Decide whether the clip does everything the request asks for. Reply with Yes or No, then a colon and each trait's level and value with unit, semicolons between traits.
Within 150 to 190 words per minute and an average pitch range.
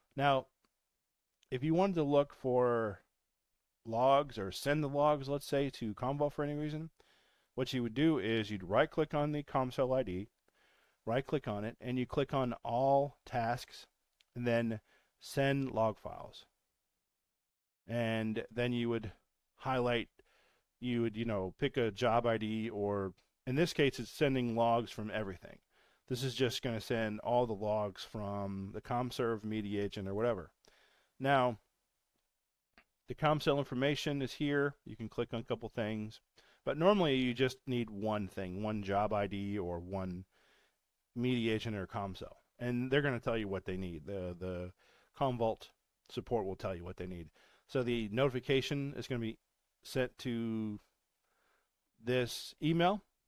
Yes: average, 160 wpm; average, 4.2 semitones